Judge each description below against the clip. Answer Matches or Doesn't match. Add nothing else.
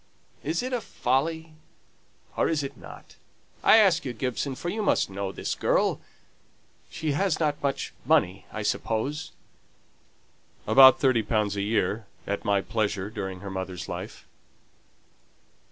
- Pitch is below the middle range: Matches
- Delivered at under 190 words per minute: Matches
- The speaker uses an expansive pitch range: Matches